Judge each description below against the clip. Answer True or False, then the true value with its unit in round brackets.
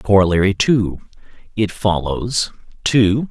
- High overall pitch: False (100 Hz)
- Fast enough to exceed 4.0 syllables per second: False (3.7 syllables/s)